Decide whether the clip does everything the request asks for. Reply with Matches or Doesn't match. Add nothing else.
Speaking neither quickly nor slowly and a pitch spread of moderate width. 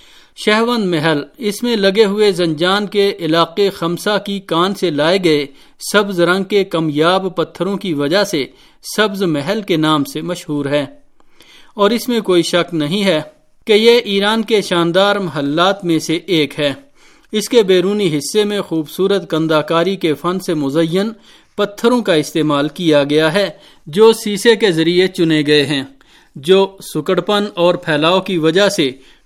Matches